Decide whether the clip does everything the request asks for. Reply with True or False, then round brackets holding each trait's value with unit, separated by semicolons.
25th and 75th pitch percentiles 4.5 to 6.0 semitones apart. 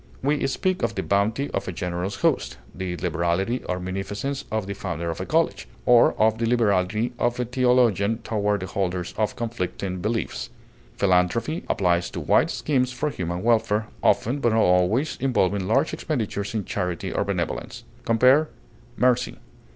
True (4.9 semitones)